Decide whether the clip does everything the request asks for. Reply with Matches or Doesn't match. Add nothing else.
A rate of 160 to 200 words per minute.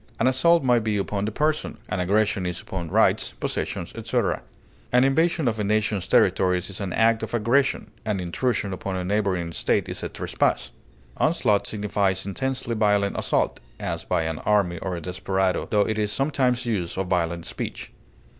Matches